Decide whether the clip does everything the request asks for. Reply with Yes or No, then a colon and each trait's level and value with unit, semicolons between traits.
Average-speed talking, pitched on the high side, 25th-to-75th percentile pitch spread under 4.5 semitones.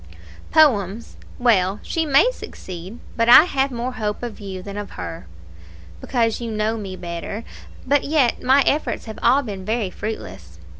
No: average, 160 wpm; high, 225 Hz; average, 4.8 semitones